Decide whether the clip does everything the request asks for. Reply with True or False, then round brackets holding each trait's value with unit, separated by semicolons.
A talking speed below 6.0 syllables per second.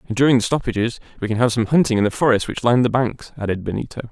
False (7.2 syllables/s)